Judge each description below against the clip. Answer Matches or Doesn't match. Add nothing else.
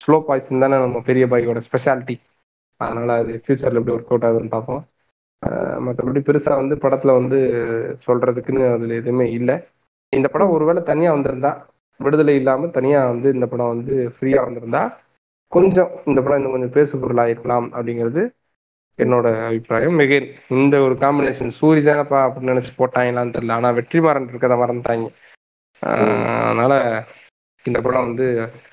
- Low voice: Matches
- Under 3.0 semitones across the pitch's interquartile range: Matches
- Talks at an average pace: Doesn't match